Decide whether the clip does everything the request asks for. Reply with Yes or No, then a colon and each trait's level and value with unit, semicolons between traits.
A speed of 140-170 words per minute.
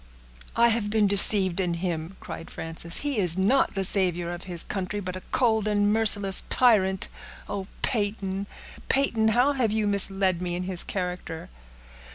Yes: average, 165 wpm